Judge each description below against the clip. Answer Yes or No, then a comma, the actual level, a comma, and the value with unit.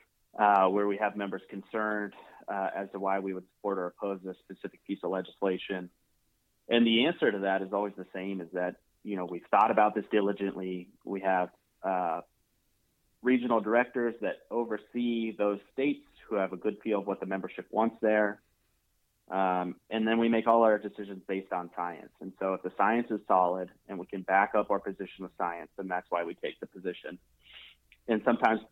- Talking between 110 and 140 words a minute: No, average, 195 wpm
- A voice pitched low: Yes, low, 100 Hz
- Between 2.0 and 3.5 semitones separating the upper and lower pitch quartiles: Yes, narrow, 2.4 semitones